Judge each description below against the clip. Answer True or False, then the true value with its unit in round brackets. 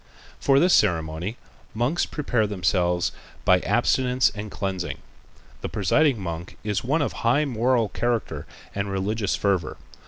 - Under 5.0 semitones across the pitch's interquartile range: False (5.4 semitones)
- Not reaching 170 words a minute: True (135 wpm)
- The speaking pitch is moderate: False (105 Hz)